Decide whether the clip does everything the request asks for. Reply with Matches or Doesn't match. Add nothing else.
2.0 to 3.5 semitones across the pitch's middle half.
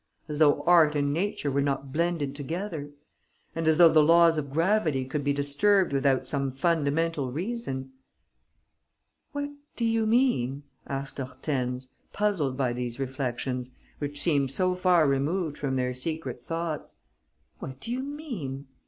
Doesn't match